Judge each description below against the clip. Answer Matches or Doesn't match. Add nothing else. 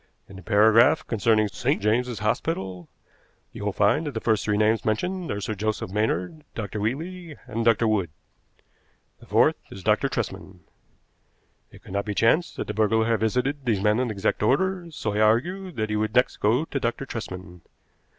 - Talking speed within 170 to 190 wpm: Matches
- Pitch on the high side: Doesn't match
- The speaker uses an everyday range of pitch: Matches